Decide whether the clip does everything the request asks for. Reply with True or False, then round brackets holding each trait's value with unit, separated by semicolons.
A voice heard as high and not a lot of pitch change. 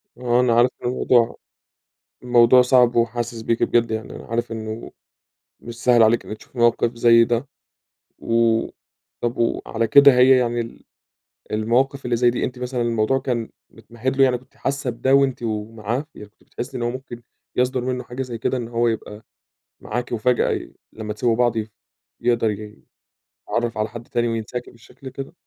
False (120 Hz; 1.6 semitones)